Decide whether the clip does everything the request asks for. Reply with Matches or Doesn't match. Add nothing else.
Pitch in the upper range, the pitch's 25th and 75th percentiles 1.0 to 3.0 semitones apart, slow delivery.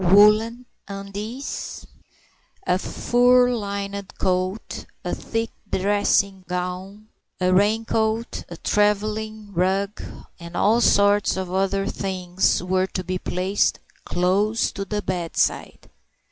Matches